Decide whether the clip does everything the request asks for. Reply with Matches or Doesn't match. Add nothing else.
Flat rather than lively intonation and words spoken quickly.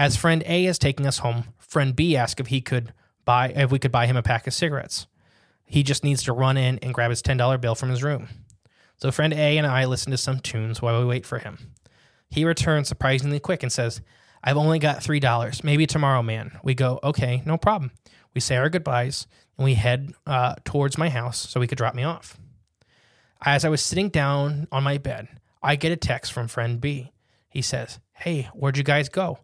Doesn't match